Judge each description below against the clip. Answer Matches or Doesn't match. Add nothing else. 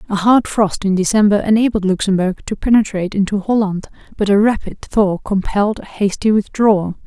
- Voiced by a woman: Matches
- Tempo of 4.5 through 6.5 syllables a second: Matches